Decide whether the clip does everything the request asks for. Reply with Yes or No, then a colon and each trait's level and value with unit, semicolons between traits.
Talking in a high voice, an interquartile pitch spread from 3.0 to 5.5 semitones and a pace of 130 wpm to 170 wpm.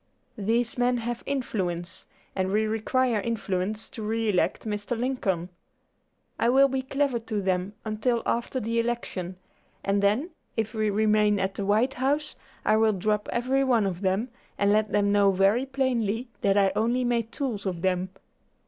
Yes: high, 220 Hz; average, 3.4 semitones; average, 165 wpm